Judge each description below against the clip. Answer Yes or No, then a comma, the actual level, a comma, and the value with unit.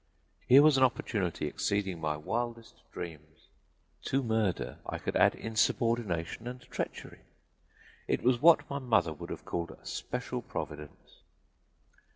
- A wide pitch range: Yes, wide, 6.7 semitones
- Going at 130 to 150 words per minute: Yes, average, 140 wpm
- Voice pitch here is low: Yes, low, 110 Hz